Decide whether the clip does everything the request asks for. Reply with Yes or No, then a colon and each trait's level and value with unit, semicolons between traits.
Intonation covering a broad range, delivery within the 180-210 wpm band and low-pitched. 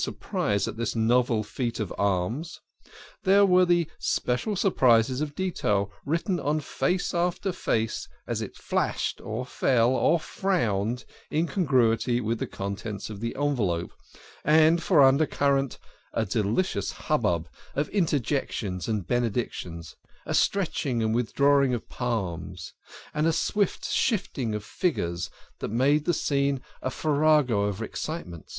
No: wide, 6.3 semitones; average, 140 wpm; low, 125 Hz